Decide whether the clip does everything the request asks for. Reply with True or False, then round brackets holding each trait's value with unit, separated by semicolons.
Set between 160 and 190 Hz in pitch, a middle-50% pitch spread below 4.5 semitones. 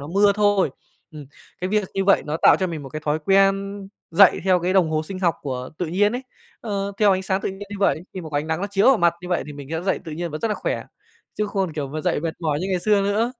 True (185 Hz; 4.0 semitones)